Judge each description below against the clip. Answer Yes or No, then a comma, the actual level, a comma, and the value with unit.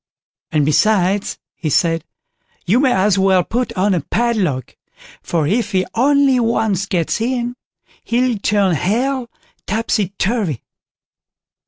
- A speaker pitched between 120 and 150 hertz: No, high, 205 Hz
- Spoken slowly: Yes, slow, 125 wpm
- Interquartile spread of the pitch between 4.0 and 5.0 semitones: Yes, average, 4.6 semitones